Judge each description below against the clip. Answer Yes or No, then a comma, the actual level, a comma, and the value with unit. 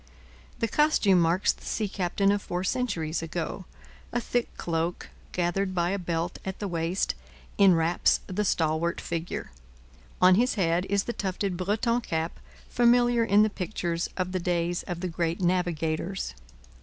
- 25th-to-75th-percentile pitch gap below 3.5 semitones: Yes, average, 3.0 semitones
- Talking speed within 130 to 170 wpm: Yes, average, 155 wpm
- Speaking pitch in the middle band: Yes, medium, 180 Hz